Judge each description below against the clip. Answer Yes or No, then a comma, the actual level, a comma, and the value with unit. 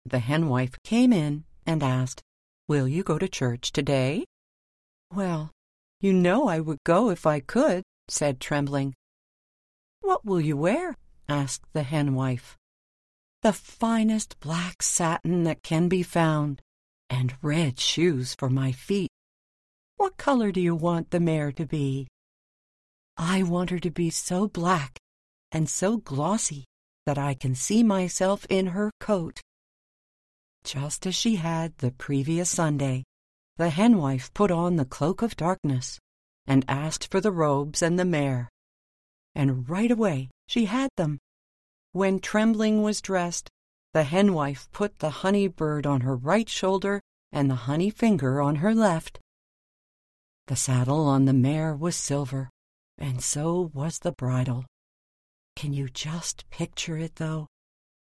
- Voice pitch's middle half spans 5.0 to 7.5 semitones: Yes, wide, 5.5 semitones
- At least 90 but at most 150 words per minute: Yes, average, 145 wpm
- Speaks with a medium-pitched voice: Yes, medium, 155 Hz